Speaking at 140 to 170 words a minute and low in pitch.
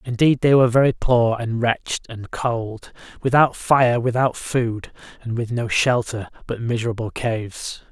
Yes: average, 150 wpm; low, 120 Hz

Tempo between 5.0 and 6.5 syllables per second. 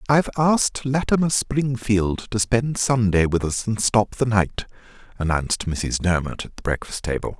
No: 4.7 syllables/s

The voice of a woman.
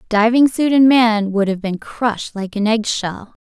Yes: female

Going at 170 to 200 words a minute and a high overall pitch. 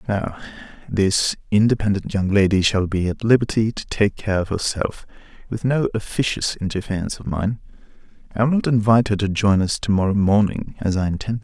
No: average, 180 wpm; low, 105 Hz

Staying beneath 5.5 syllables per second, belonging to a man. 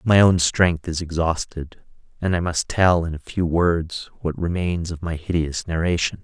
Yes: 4.4 syllables/s; male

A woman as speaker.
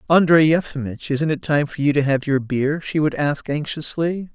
No: male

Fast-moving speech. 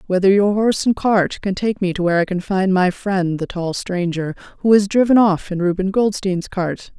Yes: fast, 225 wpm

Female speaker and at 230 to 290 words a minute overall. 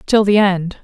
No: female; fast, 215 wpm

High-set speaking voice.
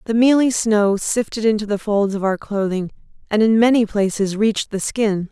Yes: high, 210 Hz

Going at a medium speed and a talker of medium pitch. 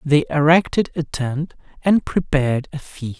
Yes: average, 150 wpm; medium, 150 Hz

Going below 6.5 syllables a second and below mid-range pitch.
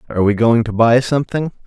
No: 6.8 syllables/s; low, 120 Hz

